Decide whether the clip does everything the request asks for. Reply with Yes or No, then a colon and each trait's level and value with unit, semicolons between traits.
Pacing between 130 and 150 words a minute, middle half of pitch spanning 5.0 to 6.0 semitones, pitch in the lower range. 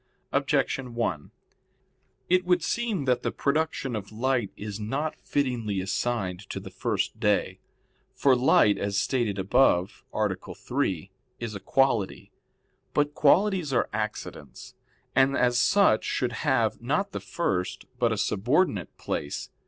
Yes: slow, 135 wpm; wide, 5.5 semitones; low, 120 Hz